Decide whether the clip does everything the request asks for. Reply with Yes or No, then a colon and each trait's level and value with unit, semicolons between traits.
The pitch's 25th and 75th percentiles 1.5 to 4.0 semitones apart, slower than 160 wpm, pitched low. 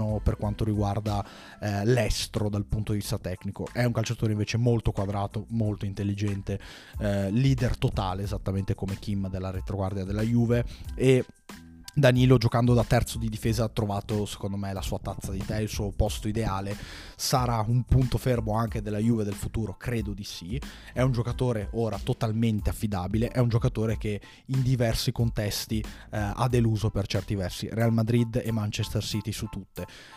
No: average, 2.7 semitones; fast, 170 wpm; low, 110 Hz